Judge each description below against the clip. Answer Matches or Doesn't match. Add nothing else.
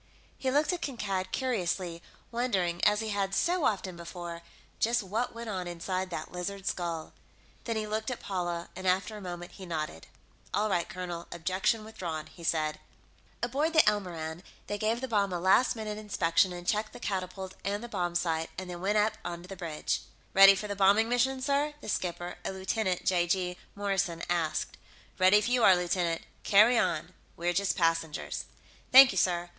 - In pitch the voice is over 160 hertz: Matches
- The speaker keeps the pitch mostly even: Doesn't match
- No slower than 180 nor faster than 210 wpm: Matches